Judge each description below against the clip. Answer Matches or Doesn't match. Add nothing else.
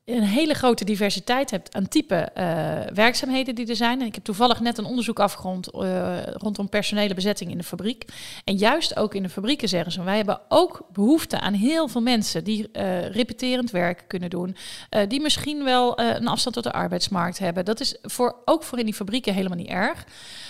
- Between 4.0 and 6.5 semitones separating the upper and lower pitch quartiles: Matches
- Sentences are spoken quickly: Matches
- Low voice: Doesn't match